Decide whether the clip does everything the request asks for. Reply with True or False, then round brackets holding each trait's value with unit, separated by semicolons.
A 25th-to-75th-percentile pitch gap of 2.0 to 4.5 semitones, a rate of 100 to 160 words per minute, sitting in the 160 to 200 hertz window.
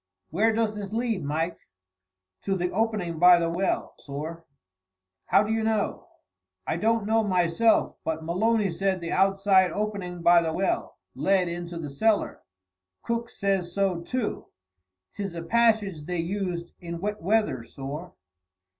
True (3.9 semitones; 145 wpm; 190 Hz)